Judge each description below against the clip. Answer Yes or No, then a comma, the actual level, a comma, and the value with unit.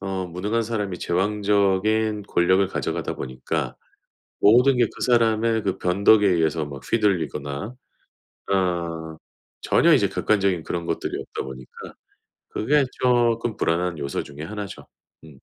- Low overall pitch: Yes, very low, 95 Hz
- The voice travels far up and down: No, average, 4.4 semitones